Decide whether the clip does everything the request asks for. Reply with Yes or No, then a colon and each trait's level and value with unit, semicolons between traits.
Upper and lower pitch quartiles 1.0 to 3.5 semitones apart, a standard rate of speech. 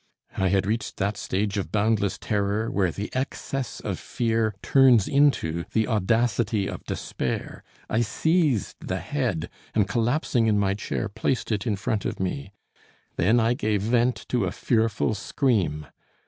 Yes: average, 3.1 semitones; average, 155 wpm